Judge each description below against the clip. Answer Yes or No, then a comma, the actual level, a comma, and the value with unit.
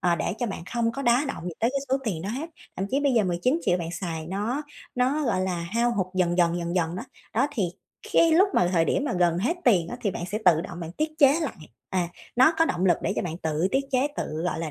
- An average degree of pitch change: No, wide, 7.0 semitones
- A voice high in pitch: Yes, high, 195 Hz